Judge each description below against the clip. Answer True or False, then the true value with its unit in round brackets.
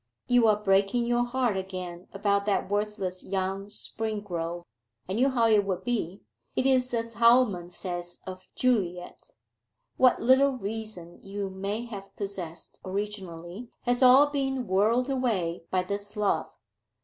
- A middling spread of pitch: True (4.4 semitones)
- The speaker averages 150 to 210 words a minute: False (140 wpm)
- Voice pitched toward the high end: True (205 Hz)